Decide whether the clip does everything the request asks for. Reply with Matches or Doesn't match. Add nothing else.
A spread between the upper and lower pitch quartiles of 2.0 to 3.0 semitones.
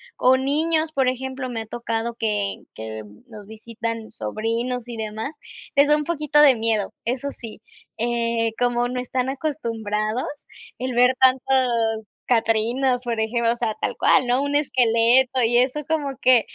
Matches